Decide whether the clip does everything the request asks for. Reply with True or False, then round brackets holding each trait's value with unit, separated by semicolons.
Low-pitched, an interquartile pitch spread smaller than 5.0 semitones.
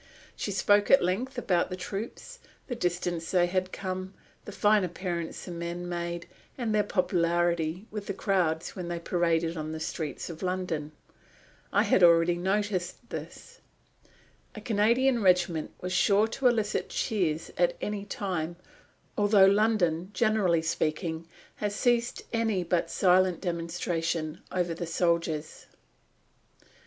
False (180 Hz; 3.3 semitones)